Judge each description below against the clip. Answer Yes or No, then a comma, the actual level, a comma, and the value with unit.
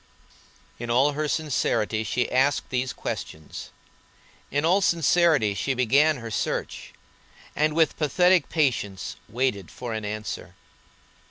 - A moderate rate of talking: No, slow, 115 wpm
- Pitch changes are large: Yes, wide, 5.7 semitones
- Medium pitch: No, low, 130 Hz